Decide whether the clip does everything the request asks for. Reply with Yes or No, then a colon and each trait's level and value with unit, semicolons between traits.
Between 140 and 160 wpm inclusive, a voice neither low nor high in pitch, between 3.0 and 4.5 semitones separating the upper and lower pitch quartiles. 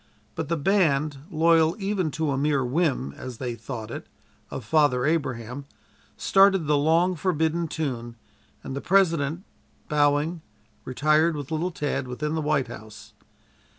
Yes: average, 150 wpm; medium, 150 Hz; average, 3.6 semitones